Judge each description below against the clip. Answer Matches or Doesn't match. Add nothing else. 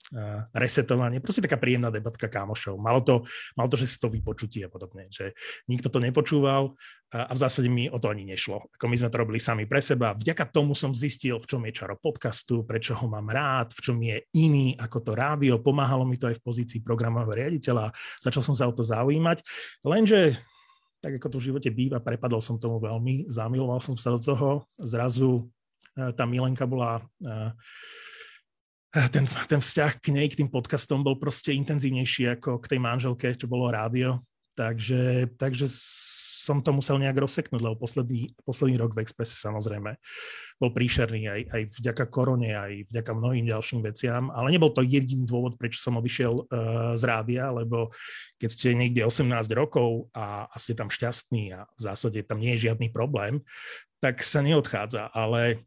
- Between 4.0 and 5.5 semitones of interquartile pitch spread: Doesn't match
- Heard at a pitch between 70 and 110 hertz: Doesn't match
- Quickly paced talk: Matches